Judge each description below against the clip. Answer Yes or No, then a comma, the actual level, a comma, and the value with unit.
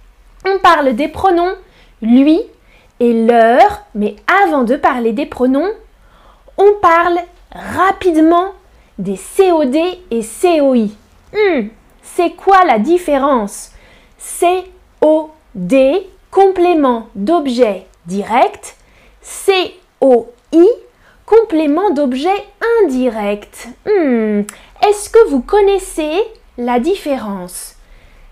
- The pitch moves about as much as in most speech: No, wide, 7.7 semitones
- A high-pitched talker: Yes, very high, 330 Hz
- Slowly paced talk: Yes, slow, 85 wpm